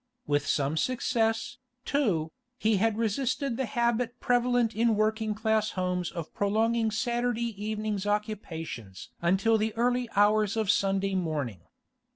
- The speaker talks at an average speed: No, slow, 130 wpm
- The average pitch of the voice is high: Yes, high, 215 Hz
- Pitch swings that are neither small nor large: Yes, average, 3.3 semitones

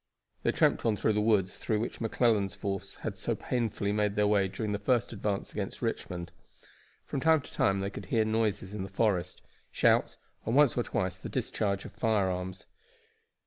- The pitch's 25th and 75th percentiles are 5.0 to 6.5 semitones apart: No, narrow, 2.4 semitones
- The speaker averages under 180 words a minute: No, average, 185 wpm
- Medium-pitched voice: No, low, 105 Hz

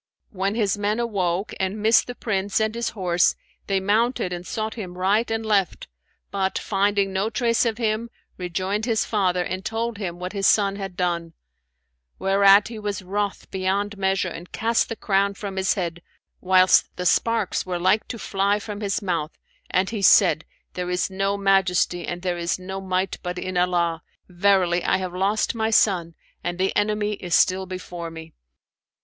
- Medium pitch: No, high, 195 Hz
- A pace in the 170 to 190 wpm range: Yes, average, 180 wpm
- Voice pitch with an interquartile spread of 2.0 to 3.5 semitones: Yes, narrow, 2.5 semitones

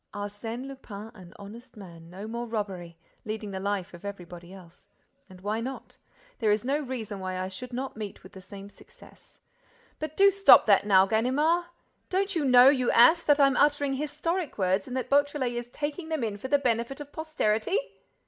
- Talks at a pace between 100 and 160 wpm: No, average, 175 wpm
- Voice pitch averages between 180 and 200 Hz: No, high, 235 Hz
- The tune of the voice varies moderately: No, wide, 6.1 semitones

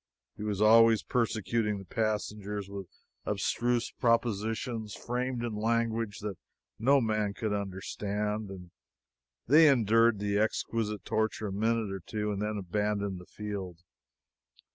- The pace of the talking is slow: Yes, slow, 130 wpm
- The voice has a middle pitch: No, low, 105 Hz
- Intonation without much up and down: Yes, narrow, 2.1 semitones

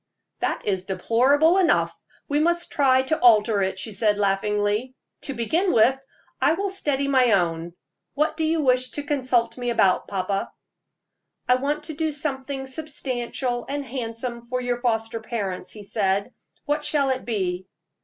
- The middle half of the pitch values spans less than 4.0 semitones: No, wide, 5.4 semitones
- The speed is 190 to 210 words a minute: No, average, 160 wpm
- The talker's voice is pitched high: Yes, very high, 250 Hz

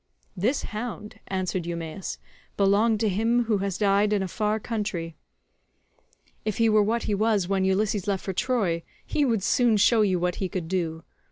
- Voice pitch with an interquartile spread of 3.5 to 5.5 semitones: No, average, 2.8 semitones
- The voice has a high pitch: Yes, high, 205 Hz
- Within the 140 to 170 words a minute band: No, average, 180 wpm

